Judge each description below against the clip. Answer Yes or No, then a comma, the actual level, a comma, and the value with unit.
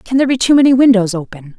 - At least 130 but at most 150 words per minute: No, fast, 265 wpm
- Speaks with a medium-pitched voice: No, high, 230 Hz